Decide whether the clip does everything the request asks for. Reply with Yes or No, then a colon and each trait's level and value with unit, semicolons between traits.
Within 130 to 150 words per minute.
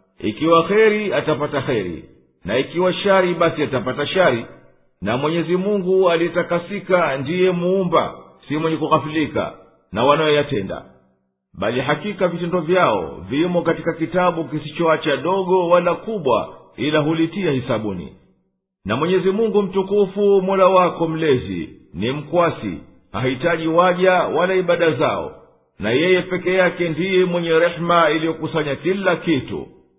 No: average, 120 wpm